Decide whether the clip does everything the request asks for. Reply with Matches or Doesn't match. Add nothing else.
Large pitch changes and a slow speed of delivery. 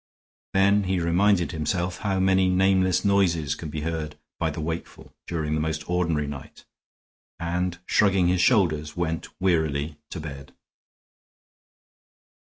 Doesn't match